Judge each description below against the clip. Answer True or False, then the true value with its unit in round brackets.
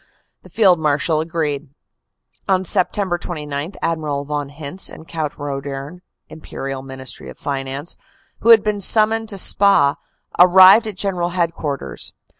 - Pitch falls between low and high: True (160 Hz)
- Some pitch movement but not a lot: True (4.8 semitones)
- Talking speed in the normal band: False (130 wpm)